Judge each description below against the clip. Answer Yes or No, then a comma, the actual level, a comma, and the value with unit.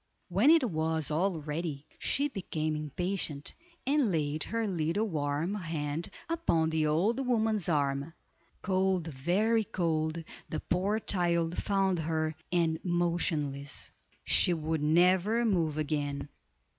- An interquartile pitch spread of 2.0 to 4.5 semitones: Yes, average, 4.0 semitones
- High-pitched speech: No, medium, 165 Hz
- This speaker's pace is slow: Yes, slow, 120 wpm